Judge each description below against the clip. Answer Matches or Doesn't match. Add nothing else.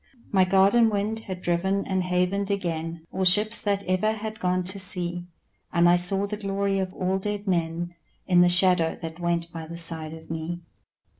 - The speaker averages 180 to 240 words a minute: Matches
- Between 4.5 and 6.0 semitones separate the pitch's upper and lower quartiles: Doesn't match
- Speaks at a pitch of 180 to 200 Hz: Matches